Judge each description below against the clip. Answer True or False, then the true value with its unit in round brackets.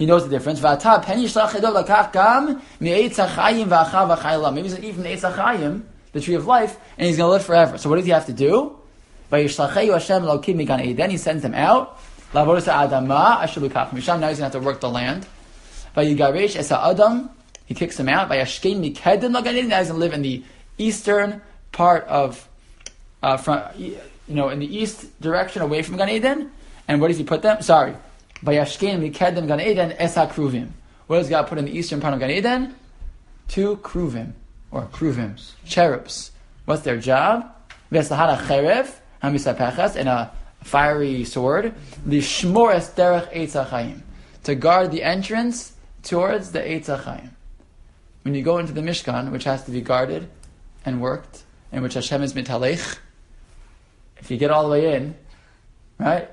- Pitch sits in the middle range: True (155 Hz)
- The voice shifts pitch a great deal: True (6.0 semitones)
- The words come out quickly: False (135 wpm)